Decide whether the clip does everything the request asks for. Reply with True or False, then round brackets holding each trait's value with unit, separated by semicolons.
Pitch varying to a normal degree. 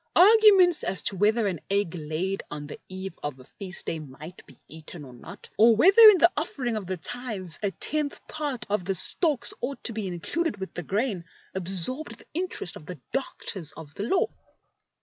False (7.6 semitones)